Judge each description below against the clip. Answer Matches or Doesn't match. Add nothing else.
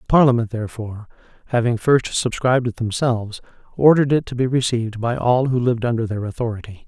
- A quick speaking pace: Doesn't match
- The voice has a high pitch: Doesn't match